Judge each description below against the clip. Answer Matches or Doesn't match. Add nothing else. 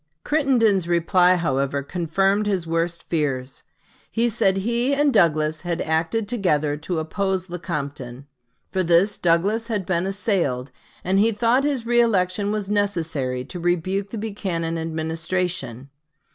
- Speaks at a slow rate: Matches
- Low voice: Doesn't match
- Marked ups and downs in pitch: Doesn't match